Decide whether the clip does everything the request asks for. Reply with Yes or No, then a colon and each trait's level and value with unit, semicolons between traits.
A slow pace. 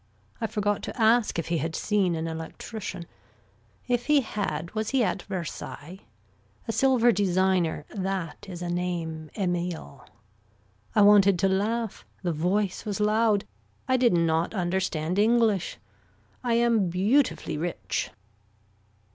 Yes: slow, 130 wpm